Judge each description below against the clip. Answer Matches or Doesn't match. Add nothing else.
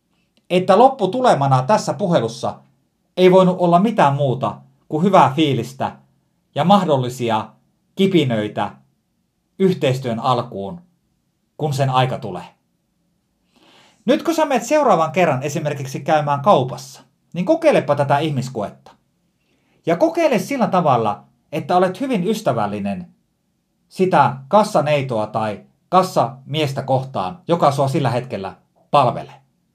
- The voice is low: Doesn't match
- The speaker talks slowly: Doesn't match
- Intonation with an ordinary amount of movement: Doesn't match